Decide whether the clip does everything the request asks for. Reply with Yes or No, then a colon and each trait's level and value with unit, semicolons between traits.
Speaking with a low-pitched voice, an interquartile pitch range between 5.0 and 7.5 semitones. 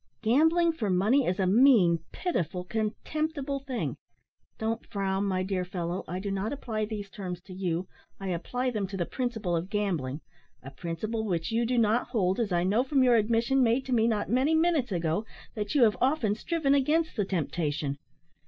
No: high, 215 Hz; wide, 5.6 semitones